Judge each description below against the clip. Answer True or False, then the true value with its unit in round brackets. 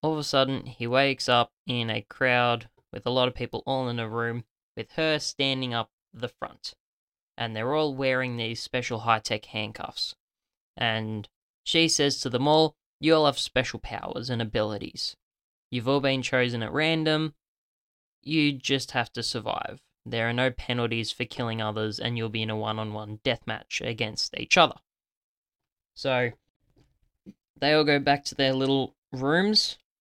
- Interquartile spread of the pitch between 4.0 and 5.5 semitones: False (3.2 semitones)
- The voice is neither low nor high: False (125 Hz)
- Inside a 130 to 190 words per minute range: True (170 wpm)